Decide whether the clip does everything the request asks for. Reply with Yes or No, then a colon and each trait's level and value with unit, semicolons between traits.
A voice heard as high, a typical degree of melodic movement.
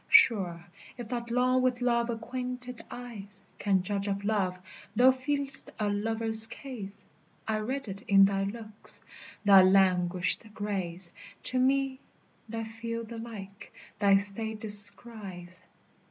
Yes: high, 220 Hz; average, 3.6 semitones